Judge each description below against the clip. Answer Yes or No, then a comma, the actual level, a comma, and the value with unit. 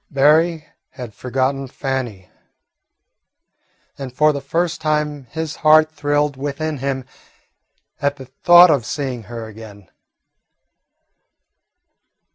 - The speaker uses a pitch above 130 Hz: Yes, medium, 140 Hz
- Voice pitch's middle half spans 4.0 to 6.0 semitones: No, average, 3.0 semitones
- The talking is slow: Yes, slow, 100 wpm